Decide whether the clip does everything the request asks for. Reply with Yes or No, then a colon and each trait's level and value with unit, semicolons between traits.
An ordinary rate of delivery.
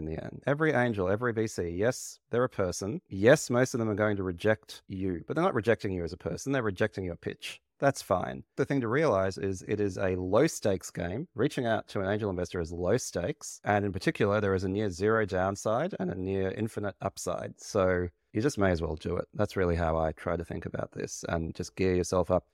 No: fast, 240 wpm